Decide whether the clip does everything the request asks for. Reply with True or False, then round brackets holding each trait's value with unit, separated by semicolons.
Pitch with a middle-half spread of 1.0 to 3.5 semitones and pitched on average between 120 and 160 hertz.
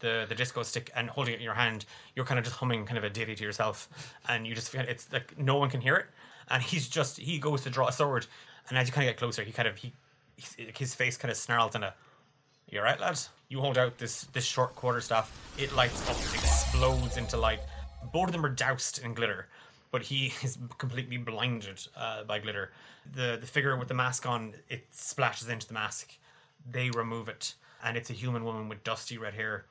True (2.6 semitones; 125 Hz)